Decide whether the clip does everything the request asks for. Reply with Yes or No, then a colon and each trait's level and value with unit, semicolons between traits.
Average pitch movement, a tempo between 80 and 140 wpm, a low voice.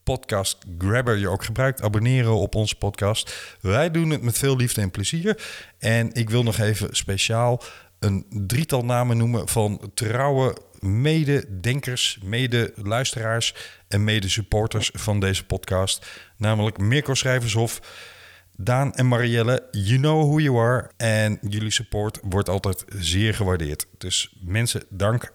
Yes: average, 3.4 semitones; slow, 135 wpm; low, 110 Hz